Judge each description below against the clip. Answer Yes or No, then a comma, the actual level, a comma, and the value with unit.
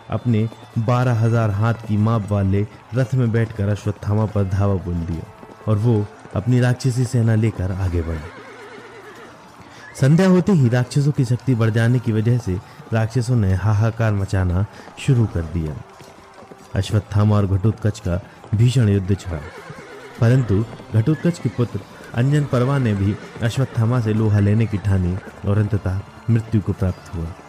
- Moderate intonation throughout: Yes, average, 3.5 semitones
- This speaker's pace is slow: No, average, 150 wpm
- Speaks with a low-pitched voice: Yes, low, 110 Hz